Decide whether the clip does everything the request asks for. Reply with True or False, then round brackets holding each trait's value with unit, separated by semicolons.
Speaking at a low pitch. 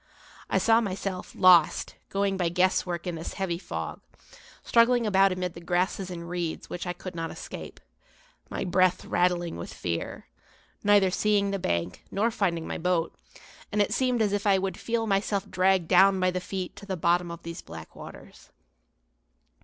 False (185 Hz)